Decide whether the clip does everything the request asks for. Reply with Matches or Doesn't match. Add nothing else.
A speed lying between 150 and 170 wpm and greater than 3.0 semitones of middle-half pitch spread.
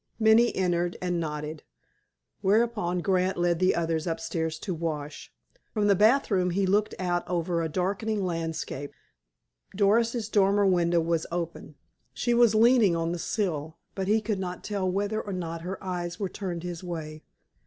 Matches